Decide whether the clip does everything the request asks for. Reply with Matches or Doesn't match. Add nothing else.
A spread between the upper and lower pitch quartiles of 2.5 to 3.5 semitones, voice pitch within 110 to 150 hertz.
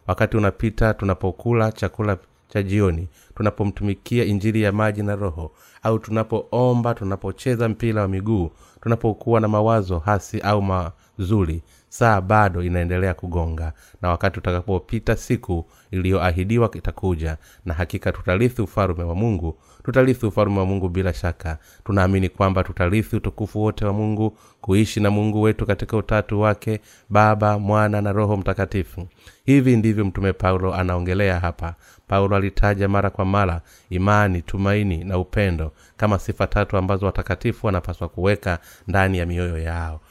Doesn't match